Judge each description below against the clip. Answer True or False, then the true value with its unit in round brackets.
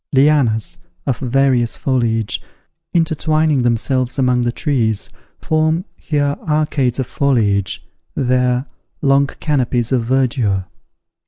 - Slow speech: True (100 wpm)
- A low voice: True (130 Hz)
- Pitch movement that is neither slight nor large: True (3.2 semitones)